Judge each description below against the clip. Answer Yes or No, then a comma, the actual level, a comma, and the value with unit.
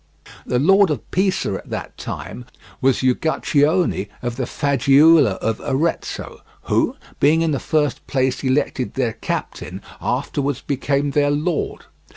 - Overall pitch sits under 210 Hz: Yes, medium, 140 Hz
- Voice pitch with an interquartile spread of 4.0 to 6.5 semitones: No, average, 3.3 semitones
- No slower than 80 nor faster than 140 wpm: Yes, slow, 135 wpm